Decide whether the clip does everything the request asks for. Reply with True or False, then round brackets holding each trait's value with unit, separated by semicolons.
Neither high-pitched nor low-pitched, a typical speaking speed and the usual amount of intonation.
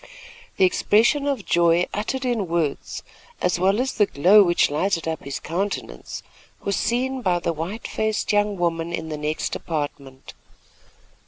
True (180 Hz; 155 wpm; 4.4 semitones)